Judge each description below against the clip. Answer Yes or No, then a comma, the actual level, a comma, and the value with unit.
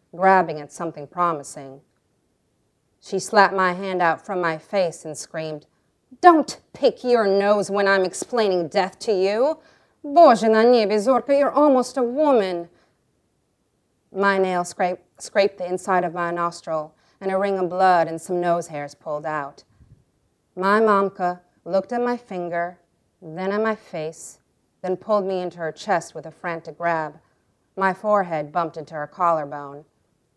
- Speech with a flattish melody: No, average, 3.8 semitones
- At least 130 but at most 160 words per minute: Yes, average, 150 wpm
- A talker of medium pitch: Yes, medium, 180 Hz